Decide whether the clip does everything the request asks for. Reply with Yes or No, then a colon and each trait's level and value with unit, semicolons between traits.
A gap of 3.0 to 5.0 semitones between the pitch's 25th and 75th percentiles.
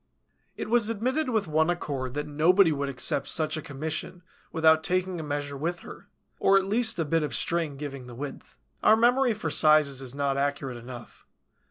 Yes: average, 4.7 semitones